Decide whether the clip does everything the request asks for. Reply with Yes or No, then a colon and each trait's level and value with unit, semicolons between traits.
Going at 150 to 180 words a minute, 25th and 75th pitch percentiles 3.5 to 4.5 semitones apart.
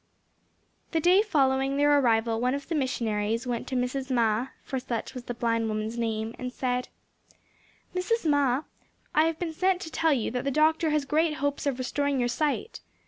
No: average, 190 wpm; average, 4.1 semitones